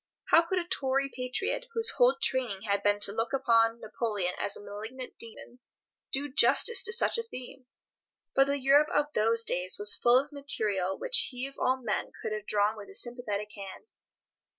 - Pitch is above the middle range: Yes, high, 245 Hz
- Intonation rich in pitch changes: No, average, 4.8 semitones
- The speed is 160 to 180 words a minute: No, average, 190 wpm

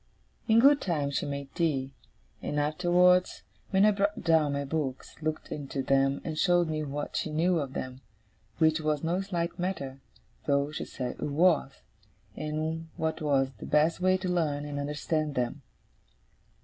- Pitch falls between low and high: Yes, medium, 155 Hz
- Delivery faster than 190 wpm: No, average, 165 wpm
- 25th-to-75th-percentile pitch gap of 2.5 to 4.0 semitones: Yes, average, 3.5 semitones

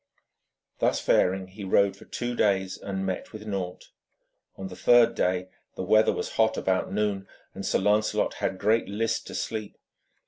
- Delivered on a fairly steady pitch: Yes, narrow, 2.2 semitones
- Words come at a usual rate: Yes, average, 170 wpm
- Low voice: Yes, low, 100 Hz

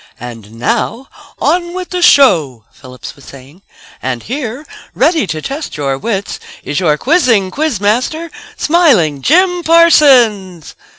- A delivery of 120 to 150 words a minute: Yes, slow, 135 wpm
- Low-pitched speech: No, high, 220 Hz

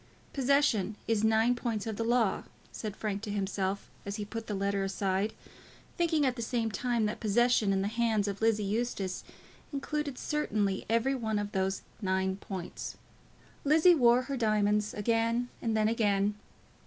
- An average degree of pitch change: Yes, average, 3.1 semitones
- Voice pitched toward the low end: No, high, 220 Hz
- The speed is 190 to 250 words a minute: No, average, 165 wpm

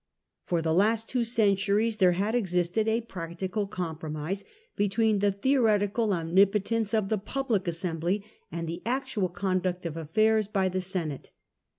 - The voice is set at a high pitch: Yes, high, 195 Hz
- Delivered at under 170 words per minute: Yes, average, 145 wpm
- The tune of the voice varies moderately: Yes, average, 3.8 semitones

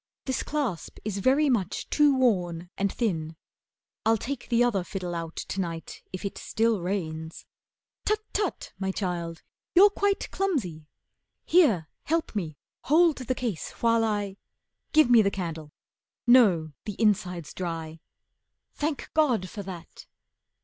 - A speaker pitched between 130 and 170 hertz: No, high, 200 Hz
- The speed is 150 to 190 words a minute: No, average, 140 wpm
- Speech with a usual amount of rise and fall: No, wide, 6.8 semitones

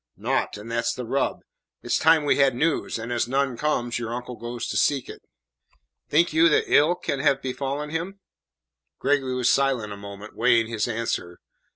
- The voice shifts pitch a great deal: No, average, 3.6 semitones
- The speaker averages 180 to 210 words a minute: Yes, average, 190 wpm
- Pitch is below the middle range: Yes, low, 125 Hz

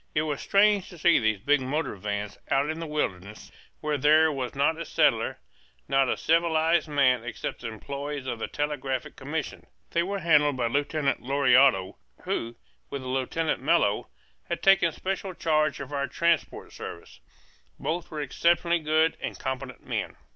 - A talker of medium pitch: Yes, medium, 145 Hz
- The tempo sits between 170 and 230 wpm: No, average, 160 wpm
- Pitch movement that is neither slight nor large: Yes, average, 3.9 semitones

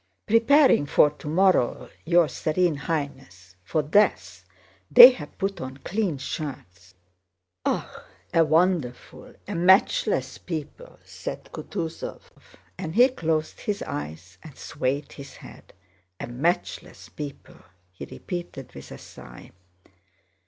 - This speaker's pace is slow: Yes, slow, 110 wpm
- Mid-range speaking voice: Yes, medium, 155 Hz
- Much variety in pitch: Yes, wide, 6.0 semitones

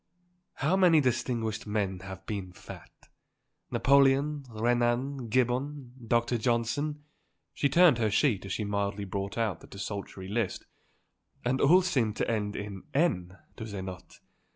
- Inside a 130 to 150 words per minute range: Yes, average, 145 wpm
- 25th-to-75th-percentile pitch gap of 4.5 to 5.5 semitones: Yes, average, 5.1 semitones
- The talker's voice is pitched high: No, low, 115 Hz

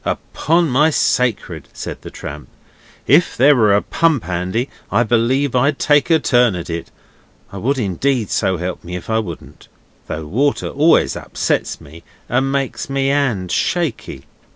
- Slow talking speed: No, average, 160 wpm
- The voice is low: Yes, low, 120 Hz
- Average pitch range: No, wide, 7.2 semitones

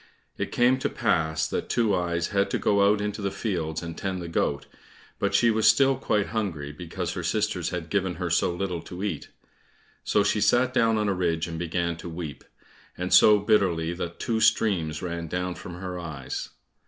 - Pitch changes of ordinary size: Yes, average, 3.8 semitones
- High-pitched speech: No, very low, 90 Hz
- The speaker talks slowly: No, average, 200 wpm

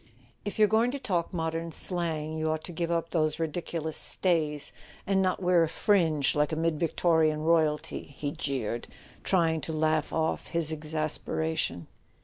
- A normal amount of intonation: No, narrow, 1.8 semitones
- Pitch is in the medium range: Yes, medium, 160 Hz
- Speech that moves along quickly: No, average, 160 wpm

